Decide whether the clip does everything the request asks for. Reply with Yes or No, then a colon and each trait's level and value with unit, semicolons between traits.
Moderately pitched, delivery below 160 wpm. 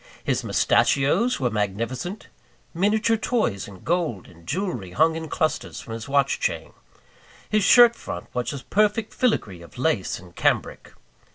Yes: medium, 145 Hz; average, 150 wpm